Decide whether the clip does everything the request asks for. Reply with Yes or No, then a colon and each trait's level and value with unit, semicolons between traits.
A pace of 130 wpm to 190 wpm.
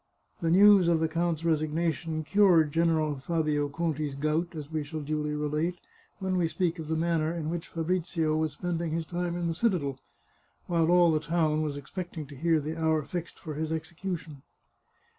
Yes: average, 180 wpm